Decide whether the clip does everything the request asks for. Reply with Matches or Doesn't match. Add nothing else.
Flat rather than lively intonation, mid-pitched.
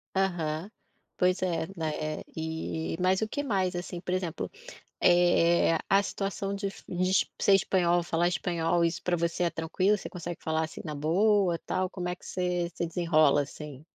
Matches